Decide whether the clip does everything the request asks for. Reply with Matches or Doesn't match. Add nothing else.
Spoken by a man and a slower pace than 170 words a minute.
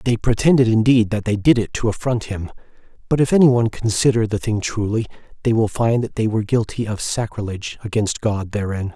Doesn't match